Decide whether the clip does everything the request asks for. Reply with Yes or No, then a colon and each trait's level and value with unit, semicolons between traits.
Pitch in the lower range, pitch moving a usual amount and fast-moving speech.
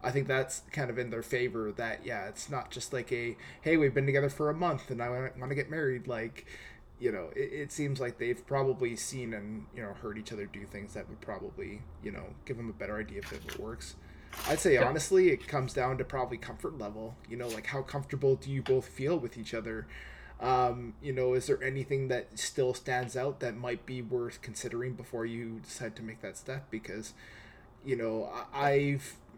Yes: low, 125 Hz; average, 3.0 semitones; fast, 225 wpm